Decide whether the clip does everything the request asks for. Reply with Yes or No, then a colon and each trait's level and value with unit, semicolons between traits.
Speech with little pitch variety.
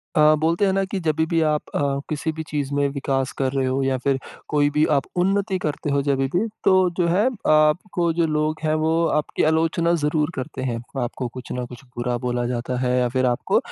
No: average, 4.0 semitones